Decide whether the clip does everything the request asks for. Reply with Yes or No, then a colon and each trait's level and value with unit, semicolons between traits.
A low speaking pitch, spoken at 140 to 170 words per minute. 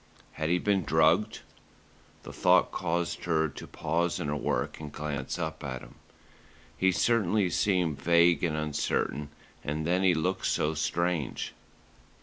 Yes: very low, 80 Hz; average, 145 wpm